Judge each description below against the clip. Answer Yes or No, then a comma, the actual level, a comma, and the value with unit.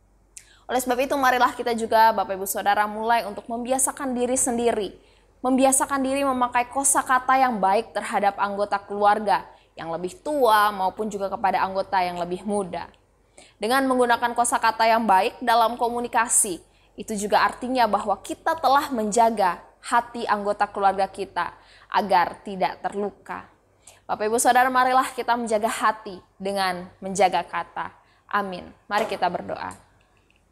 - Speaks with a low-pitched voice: No, high, 215 Hz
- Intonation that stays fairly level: No, average, 4.2 semitones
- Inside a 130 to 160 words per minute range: Yes, average, 135 wpm